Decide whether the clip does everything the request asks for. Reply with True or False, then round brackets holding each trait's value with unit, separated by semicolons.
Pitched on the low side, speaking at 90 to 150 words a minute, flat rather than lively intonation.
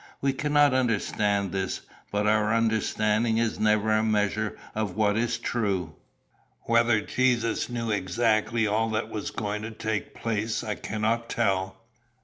True (110 Hz; 140 wpm; 1.8 semitones)